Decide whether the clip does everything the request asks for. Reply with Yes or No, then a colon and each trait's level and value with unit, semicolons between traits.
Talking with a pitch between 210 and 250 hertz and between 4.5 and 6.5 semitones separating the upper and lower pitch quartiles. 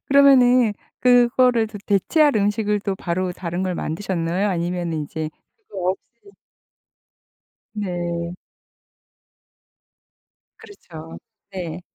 No: high, 190 Hz; average, 5.2 semitones